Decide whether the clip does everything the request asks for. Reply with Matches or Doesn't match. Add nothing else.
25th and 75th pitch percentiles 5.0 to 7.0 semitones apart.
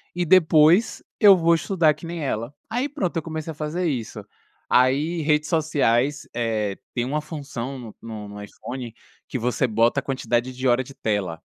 Matches